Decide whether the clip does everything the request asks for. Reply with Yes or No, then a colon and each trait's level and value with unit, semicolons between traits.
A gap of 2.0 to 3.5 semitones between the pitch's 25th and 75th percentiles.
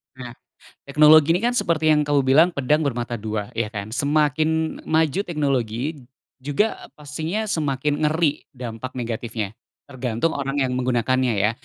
No: average, 4.3 semitones